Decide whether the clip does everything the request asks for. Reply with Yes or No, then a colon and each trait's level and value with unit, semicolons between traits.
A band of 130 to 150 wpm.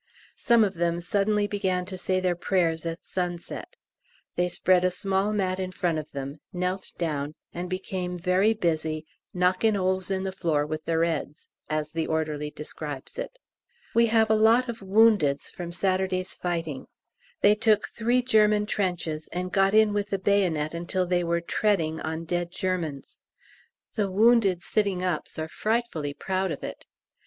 No: average, 165 wpm